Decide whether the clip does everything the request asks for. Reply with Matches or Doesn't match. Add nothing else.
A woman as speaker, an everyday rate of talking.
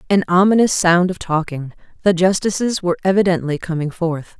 Matches